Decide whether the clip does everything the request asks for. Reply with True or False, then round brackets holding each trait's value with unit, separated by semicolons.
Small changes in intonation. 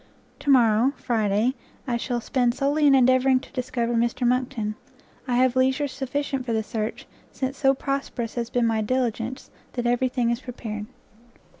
True (2.1 semitones)